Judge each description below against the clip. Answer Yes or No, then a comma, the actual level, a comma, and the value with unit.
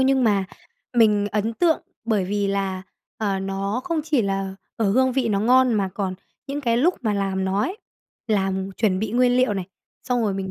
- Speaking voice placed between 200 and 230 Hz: Yes, high, 210 Hz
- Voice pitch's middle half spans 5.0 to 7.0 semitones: No, average, 4.2 semitones